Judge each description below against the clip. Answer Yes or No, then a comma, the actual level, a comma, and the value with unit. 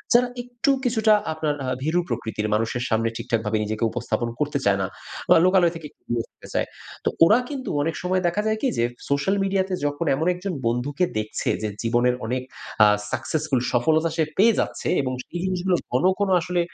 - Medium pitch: Yes, medium, 155 Hz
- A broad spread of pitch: Yes, wide, 7.6 semitones